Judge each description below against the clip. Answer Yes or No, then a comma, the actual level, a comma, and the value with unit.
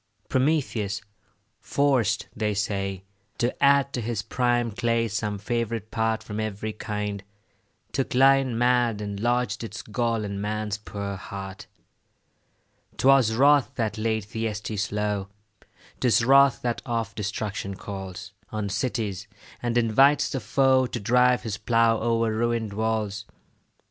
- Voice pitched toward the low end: Yes, low, 110 Hz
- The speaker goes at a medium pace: No, slow, 130 wpm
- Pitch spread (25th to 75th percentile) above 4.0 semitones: No, average, 2.8 semitones